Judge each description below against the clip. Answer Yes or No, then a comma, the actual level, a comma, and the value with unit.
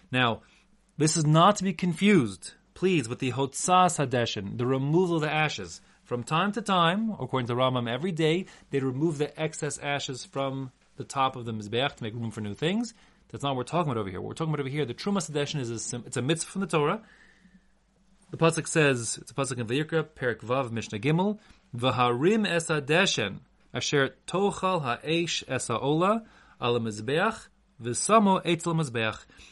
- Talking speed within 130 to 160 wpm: No, average, 185 wpm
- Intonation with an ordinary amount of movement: No, wide, 6.1 semitones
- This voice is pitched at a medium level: Yes, medium, 150 Hz